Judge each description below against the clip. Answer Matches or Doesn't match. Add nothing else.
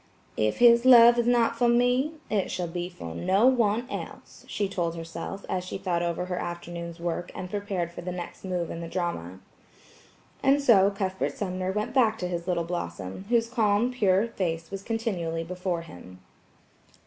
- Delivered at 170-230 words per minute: Matches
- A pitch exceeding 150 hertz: Matches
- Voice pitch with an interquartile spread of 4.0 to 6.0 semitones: Matches